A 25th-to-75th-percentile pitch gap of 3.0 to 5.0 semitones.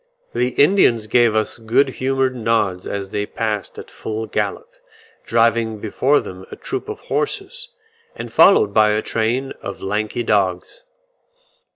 Yes: average, 3.9 semitones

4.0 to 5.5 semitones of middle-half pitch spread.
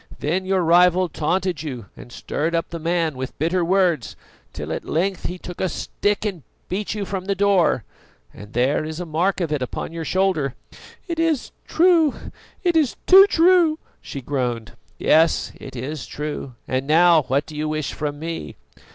Yes: average, 4.5 semitones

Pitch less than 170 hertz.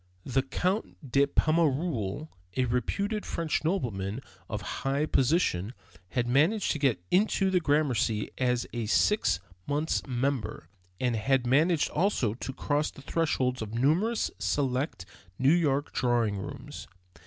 Yes: low, 135 Hz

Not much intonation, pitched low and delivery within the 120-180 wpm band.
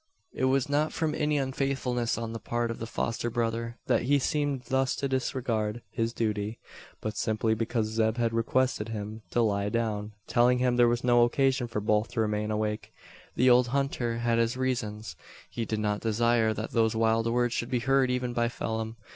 No: narrow, 2.2 semitones; low, 115 Hz; average, 195 wpm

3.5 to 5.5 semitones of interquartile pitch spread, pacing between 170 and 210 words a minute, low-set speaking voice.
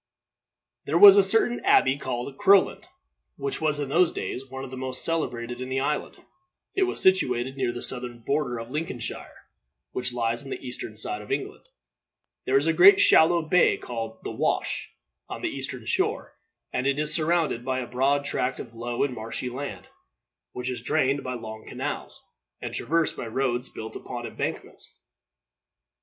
Yes: average, 3.9 semitones; average, 175 wpm; low, 130 Hz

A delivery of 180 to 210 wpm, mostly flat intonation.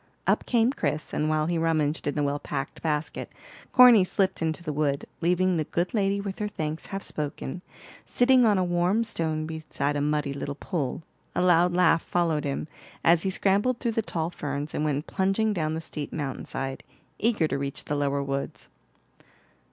No: average, 190 wpm; average, 4.4 semitones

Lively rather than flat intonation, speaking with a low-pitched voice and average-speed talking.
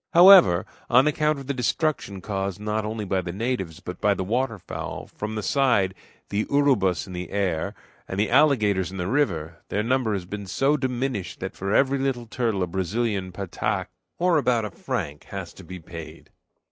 Yes: wide, 5.7 semitones; low, 105 Hz; average, 190 wpm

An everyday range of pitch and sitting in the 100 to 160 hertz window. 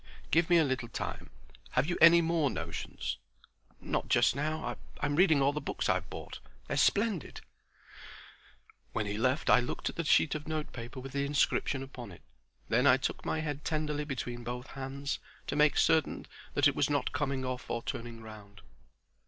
Yes: average, 3.8 semitones; medium, 140 Hz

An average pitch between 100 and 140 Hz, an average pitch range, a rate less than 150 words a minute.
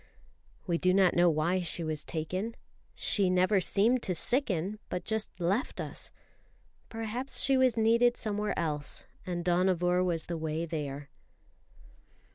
No: medium, 185 Hz; average, 4.5 semitones; average, 140 wpm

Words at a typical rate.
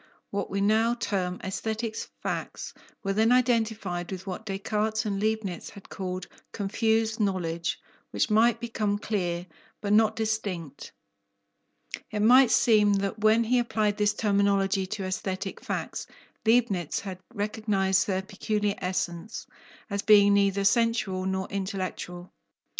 No: slow, 130 wpm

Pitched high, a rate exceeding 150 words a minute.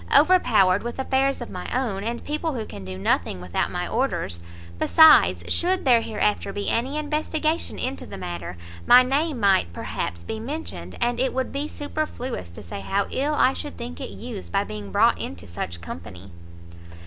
Yes: high, 230 Hz; average, 180 wpm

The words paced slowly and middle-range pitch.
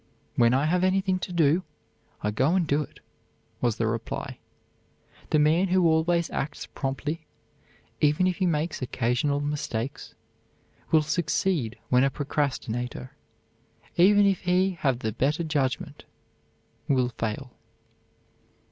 Yes: slow, 130 wpm; medium, 150 Hz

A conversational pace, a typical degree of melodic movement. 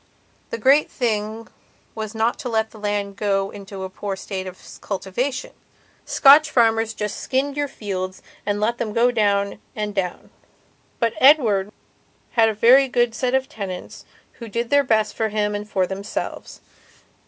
Yes: average, 165 wpm; average, 3.1 semitones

